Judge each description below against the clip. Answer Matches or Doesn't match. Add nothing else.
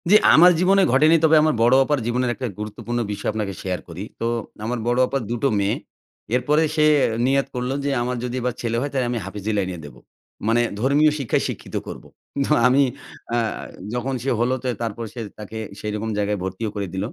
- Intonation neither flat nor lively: Matches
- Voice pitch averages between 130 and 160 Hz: Doesn't match